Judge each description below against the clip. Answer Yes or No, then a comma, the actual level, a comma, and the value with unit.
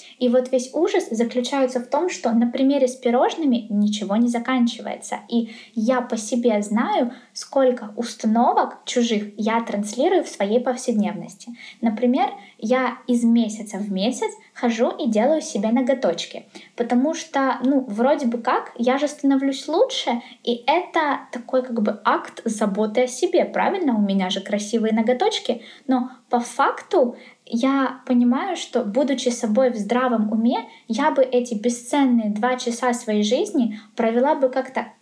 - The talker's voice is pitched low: No, high, 245 Hz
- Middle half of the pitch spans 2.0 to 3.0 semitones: Yes, narrow, 2.6 semitones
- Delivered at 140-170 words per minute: Yes, average, 145 wpm